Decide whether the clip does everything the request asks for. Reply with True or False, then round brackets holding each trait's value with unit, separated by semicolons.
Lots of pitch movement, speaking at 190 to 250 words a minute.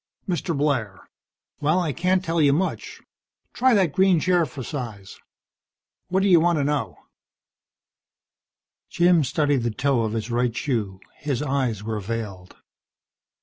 False (6.9 semitones; 145 wpm)